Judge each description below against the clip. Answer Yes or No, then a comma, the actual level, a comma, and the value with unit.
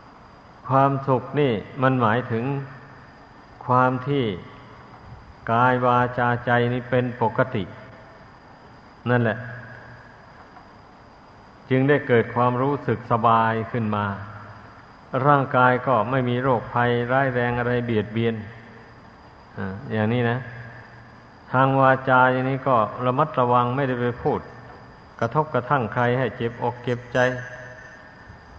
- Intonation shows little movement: Yes, narrow, 2.0 semitones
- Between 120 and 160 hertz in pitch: Yes, low, 125 Hz